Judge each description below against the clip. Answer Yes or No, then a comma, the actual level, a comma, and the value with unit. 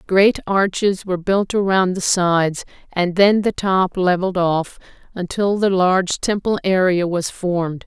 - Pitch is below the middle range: No, medium, 185 Hz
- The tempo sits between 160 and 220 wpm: No, average, 150 wpm